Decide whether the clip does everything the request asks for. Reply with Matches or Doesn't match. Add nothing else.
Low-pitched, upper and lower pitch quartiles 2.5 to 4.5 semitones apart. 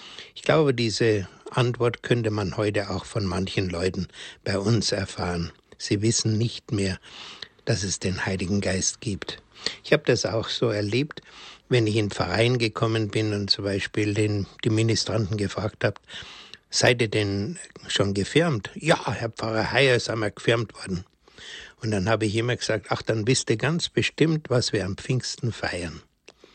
Matches